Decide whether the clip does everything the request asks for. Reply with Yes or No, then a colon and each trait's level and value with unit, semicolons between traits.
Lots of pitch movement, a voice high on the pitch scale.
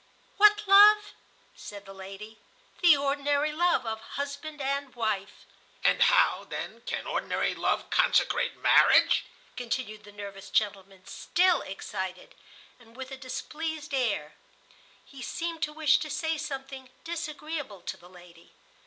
Yes: wide, 7.1 semitones; very high, 275 Hz